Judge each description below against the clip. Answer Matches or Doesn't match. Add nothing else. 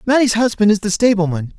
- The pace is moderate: Matches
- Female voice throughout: Doesn't match